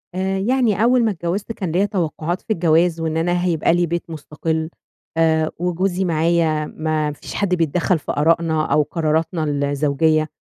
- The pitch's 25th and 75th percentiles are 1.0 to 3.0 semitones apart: Yes, narrow, 2.5 semitones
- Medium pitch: Yes, medium, 165 Hz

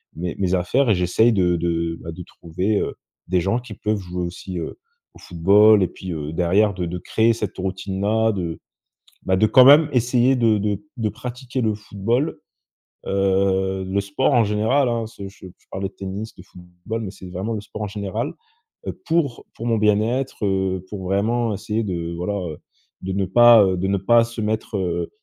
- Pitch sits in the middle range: No, low, 100 Hz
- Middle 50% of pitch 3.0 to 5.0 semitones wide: Yes, average, 3.4 semitones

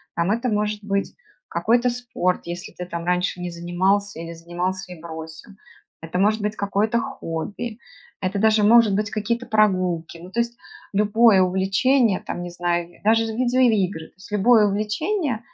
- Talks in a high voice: Yes, high, 200 Hz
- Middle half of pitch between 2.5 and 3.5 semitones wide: No, average, 4.0 semitones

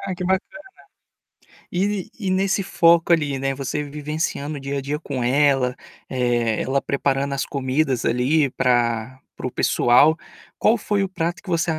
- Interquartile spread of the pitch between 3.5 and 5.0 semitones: Yes, average, 4.5 semitones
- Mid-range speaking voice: Yes, medium, 145 Hz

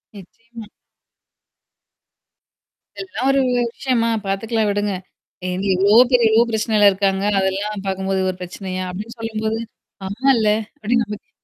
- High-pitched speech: Yes, high, 210 Hz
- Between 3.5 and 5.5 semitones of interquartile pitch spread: No, average, 3.0 semitones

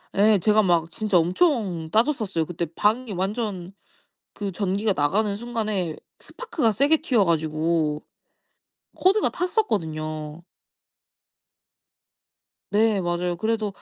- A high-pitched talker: Yes, high, 200 Hz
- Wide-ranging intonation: No, average, 4.7 semitones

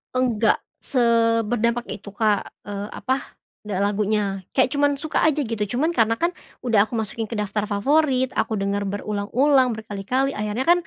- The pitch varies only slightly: No, average, 4.0 semitones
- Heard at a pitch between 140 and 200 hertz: No, high, 225 Hz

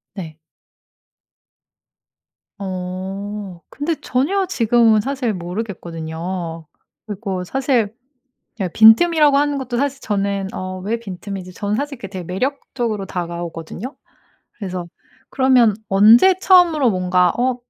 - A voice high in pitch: Yes, high, 210 Hz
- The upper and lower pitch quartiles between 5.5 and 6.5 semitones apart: Yes, wide, 5.9 semitones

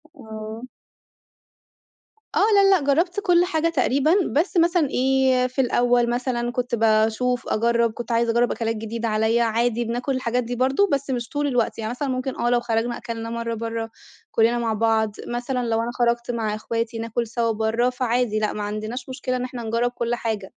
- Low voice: No, high, 240 Hz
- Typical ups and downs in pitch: No, narrow, 2.0 semitones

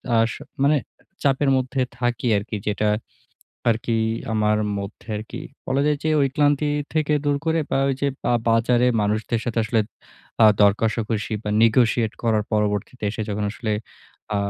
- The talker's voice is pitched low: Yes, low, 115 Hz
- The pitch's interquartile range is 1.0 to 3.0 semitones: No, average, 3.9 semitones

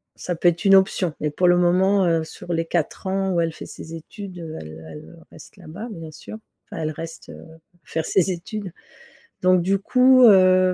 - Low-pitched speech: No, medium, 180 Hz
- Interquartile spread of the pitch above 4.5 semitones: No, average, 2.8 semitones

